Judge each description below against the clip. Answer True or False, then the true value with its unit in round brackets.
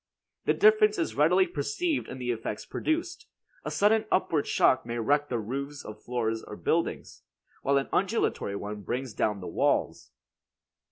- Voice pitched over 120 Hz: True (140 Hz)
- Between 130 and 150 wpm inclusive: False (160 wpm)